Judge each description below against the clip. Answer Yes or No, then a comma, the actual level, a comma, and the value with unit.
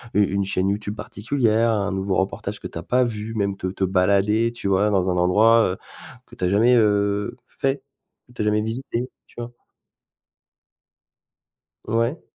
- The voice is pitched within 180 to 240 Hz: No, low, 105 Hz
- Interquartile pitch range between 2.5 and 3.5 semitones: Yes, average, 2.9 semitones